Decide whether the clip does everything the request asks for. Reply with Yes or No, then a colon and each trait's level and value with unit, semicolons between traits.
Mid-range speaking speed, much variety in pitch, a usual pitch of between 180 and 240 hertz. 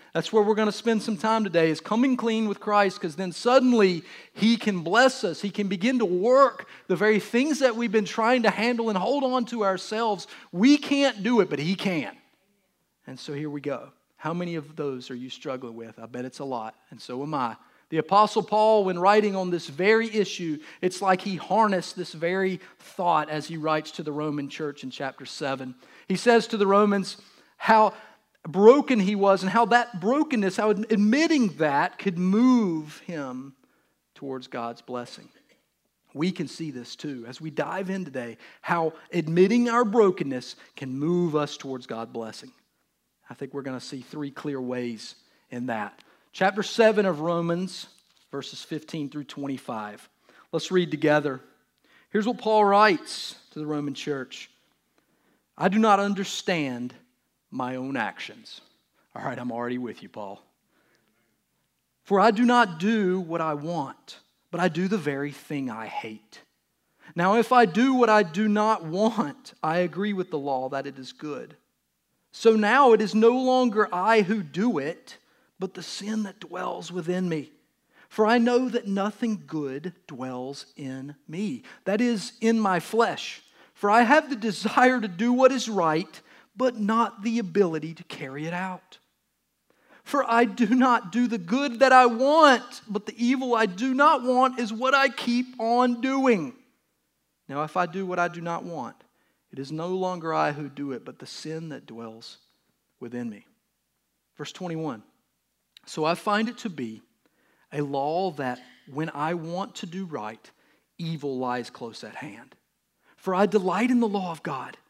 Yes: average, 180 wpm; wide, 7.1 semitones; high, 190 Hz